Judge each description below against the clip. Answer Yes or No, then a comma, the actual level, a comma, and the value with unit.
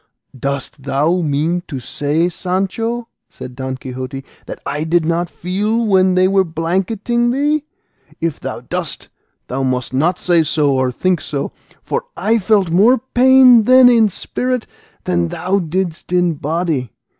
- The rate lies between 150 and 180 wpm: Yes, average, 155 wpm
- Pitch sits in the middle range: Yes, medium, 175 Hz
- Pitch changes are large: Yes, wide, 6.7 semitones